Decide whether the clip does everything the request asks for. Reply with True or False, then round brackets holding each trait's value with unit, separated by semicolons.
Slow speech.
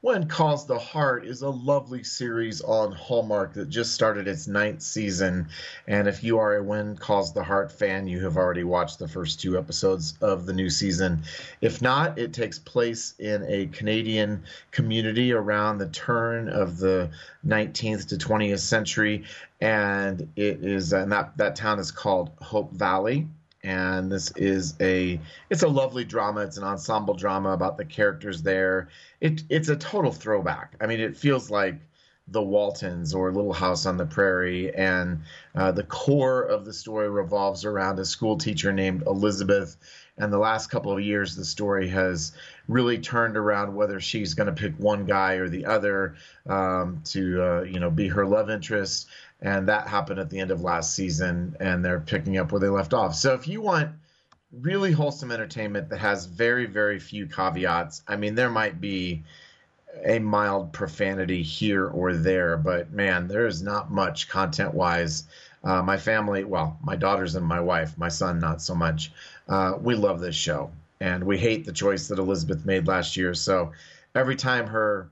False (180 wpm)